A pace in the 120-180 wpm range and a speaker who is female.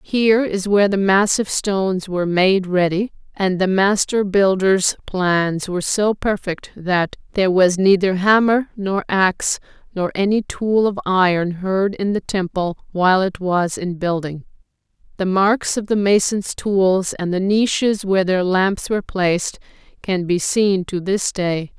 Yes: average, 160 wpm; female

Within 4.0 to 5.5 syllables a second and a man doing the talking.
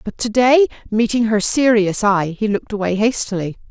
No: 5.2 syllables/s; female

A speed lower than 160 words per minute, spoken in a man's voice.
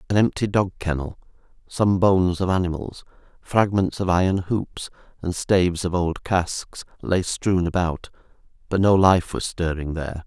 Yes: average, 150 wpm; male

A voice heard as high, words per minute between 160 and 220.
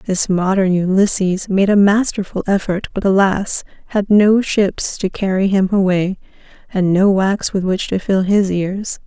Yes: high, 195 Hz; average, 165 wpm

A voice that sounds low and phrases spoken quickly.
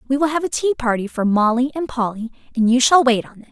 No: very high, 250 Hz; fast, 275 wpm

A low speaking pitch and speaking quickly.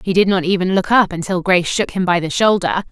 No: medium, 185 Hz; fast, 270 wpm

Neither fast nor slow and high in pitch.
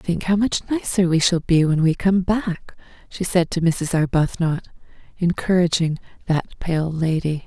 No: average, 160 wpm; medium, 170 Hz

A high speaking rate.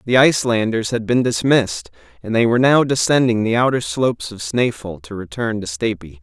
No: average, 185 wpm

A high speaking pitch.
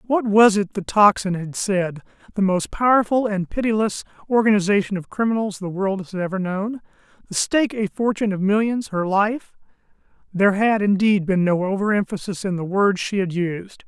Yes: high, 200 Hz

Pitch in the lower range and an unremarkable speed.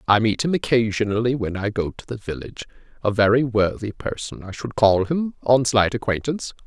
Yes: low, 115 Hz; average, 190 wpm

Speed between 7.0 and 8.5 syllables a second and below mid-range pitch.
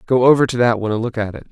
Yes: 8.2 syllables/s; low, 120 Hz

